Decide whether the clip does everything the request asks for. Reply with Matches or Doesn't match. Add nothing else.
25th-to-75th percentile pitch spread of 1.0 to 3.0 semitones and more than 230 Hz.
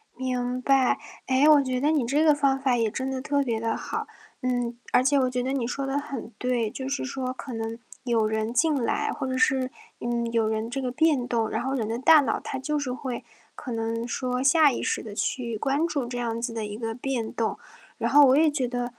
Matches